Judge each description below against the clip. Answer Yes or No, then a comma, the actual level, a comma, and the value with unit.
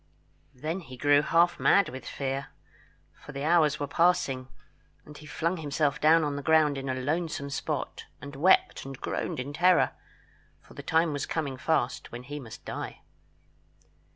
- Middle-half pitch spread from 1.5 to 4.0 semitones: Yes, average, 2.9 semitones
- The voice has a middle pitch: Yes, medium, 145 Hz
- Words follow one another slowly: No, average, 170 wpm